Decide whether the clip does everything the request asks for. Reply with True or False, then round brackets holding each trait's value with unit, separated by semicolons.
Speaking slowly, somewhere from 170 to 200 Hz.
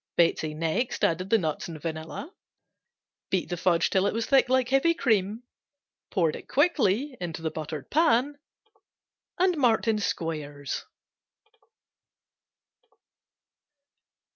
True (115 wpm; 190 Hz)